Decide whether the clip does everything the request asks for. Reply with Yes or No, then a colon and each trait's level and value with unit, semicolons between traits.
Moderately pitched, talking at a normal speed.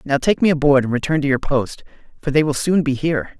No: medium, 145 Hz; fast, 265 wpm